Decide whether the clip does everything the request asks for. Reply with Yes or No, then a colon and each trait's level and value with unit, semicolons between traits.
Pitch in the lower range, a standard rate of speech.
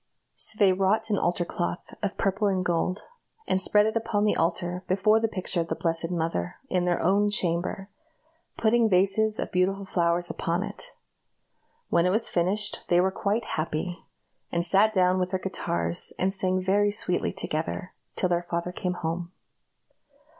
No: medium, 185 Hz; average, 170 wpm